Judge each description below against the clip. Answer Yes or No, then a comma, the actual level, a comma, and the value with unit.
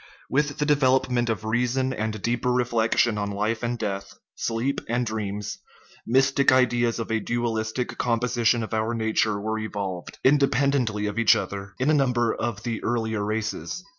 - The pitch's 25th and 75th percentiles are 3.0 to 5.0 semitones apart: No, narrow, 2.4 semitones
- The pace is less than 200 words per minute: Yes, average, 165 wpm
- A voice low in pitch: Yes, low, 115 Hz